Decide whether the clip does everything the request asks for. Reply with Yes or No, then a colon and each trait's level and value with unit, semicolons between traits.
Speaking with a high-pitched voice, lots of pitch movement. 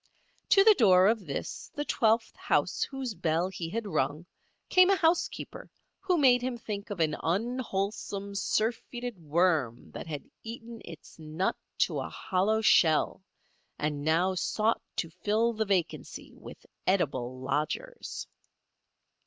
Yes: high, 200 Hz; wide, 6.2 semitones